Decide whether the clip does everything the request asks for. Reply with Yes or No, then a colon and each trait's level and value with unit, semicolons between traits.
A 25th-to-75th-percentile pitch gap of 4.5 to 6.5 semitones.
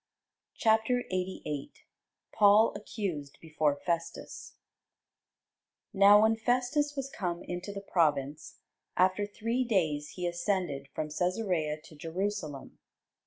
Yes: average, 5.3 semitones